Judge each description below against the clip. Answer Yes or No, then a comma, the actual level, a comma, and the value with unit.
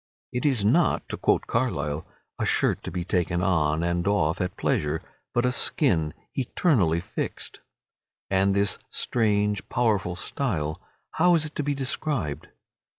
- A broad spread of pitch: Yes, wide, 6.8 semitones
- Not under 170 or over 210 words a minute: No, average, 150 wpm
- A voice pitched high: No, low, 100 Hz